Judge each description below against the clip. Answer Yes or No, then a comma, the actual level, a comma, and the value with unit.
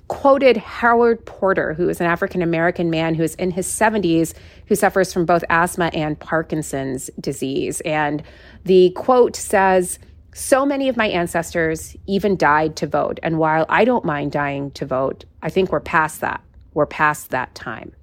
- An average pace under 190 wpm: Yes, average, 175 wpm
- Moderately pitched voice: Yes, medium, 170 Hz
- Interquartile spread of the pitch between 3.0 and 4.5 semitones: Yes, average, 3.9 semitones